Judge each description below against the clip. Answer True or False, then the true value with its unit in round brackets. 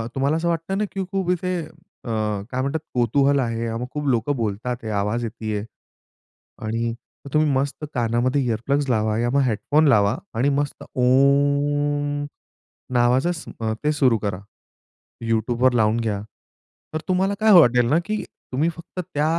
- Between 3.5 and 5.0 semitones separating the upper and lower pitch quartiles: True (4.1 semitones)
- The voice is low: True (130 Hz)